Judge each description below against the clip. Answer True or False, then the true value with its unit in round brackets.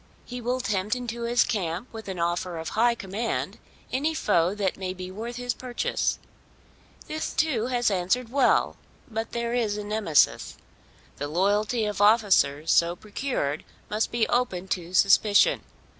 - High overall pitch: True (210 Hz)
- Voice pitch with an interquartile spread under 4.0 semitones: False (4.5 semitones)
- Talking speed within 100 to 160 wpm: True (155 wpm)